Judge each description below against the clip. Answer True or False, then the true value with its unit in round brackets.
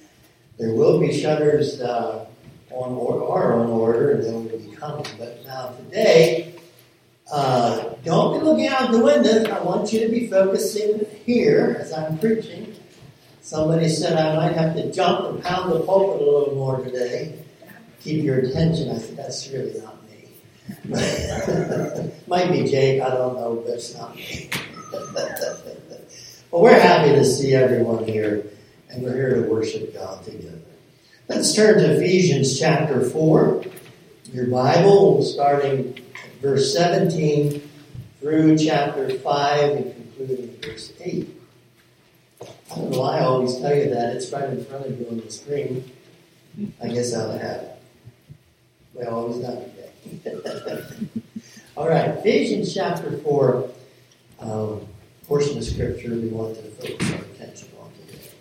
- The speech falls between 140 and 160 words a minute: True (150 wpm)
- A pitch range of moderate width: False (6.1 semitones)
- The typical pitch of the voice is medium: True (145 Hz)